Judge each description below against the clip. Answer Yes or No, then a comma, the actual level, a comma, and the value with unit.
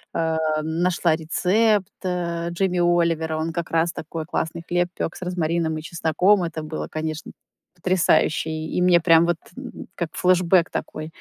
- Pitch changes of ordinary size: No, narrow, 1.8 semitones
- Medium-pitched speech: Yes, medium, 170 Hz